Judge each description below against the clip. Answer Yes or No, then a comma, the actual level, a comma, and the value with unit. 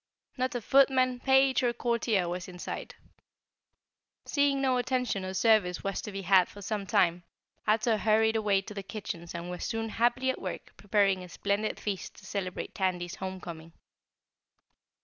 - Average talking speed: Yes, average, 165 wpm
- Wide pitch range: No, average, 4.2 semitones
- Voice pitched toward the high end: Yes, high, 205 Hz